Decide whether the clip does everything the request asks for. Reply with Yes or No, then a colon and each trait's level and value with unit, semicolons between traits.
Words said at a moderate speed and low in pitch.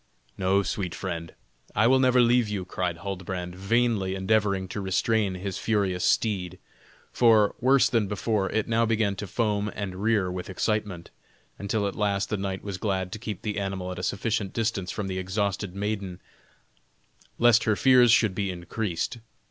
Yes: average, 170 wpm; low, 100 Hz